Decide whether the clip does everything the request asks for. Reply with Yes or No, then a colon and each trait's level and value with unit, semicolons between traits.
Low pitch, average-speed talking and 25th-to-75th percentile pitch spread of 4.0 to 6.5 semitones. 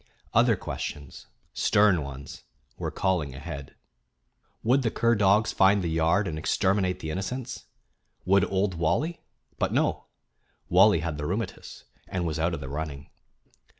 Yes: very low, 90 Hz; average, 145 wpm; average, 4.6 semitones